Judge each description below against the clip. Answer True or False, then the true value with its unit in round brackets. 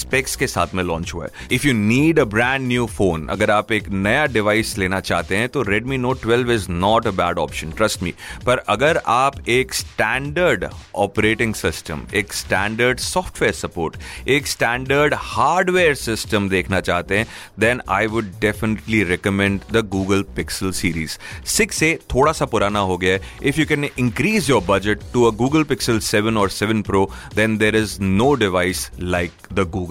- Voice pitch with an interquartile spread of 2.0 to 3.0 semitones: False (4.3 semitones)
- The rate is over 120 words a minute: True (175 wpm)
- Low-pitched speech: True (105 Hz)